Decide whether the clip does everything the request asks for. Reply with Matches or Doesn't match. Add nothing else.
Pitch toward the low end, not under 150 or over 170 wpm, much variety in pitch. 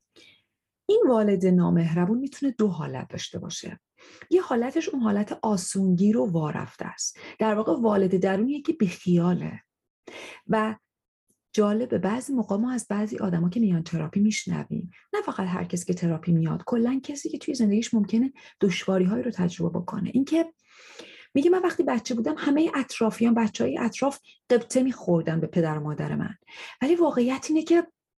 Doesn't match